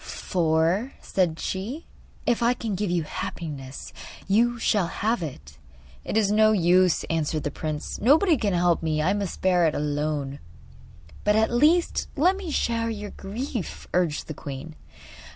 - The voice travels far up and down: Yes, wide, 6.3 semitones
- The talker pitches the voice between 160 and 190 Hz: Yes, medium, 185 Hz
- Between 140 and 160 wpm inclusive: Yes, average, 155 wpm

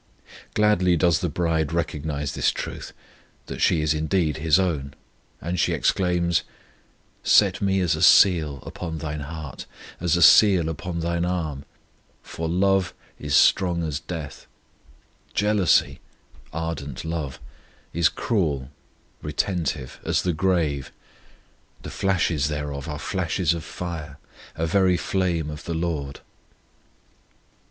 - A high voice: No, very low, 80 Hz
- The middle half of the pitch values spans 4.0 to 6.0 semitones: No, average, 2.9 semitones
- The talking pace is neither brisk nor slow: No, slow, 125 wpm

